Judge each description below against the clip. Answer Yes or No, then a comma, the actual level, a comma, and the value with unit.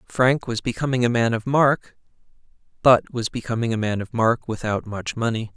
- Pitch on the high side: No, low, 115 Hz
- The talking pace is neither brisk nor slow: Yes, average, 175 wpm